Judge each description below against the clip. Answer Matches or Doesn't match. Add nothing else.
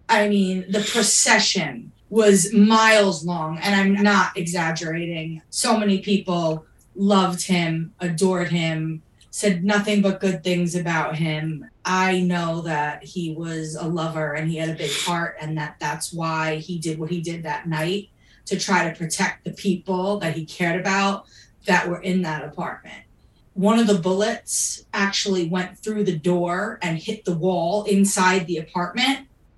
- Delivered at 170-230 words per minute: Doesn't match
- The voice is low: Doesn't match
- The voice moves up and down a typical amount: Matches